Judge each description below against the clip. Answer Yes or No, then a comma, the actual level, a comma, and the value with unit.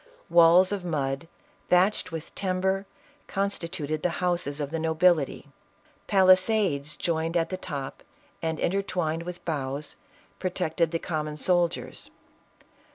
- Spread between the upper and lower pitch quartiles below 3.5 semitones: Yes, average, 2.9 semitones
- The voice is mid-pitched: Yes, medium, 170 Hz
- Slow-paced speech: Yes, slow, 120 wpm